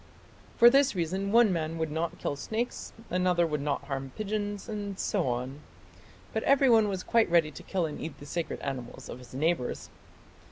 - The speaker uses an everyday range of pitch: No, wide, 5.9 semitones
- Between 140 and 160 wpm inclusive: No, average, 185 wpm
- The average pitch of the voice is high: No, medium, 170 Hz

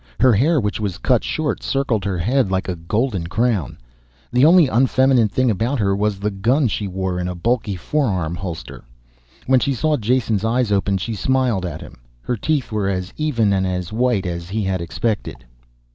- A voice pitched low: Yes, low, 105 Hz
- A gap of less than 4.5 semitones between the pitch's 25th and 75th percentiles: No, average, 5.1 semitones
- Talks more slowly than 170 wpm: No, average, 190 wpm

